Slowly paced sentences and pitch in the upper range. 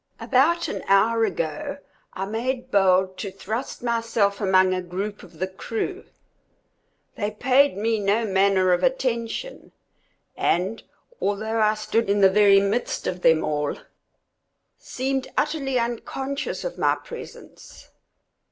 Yes: slow, 130 wpm; high, 215 Hz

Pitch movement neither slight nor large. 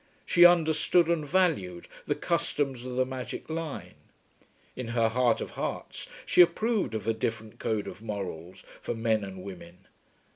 No: wide, 6.9 semitones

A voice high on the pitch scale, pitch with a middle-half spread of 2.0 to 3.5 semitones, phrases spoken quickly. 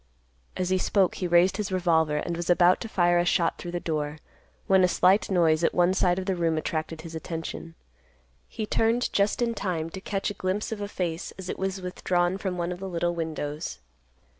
No: medium, 180 Hz; narrow, 2.4 semitones; fast, 215 wpm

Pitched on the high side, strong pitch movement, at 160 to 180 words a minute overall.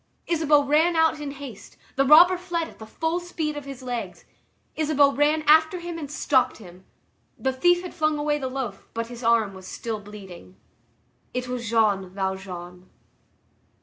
Yes: very high, 275 Hz; wide, 6.1 semitones; average, 170 wpm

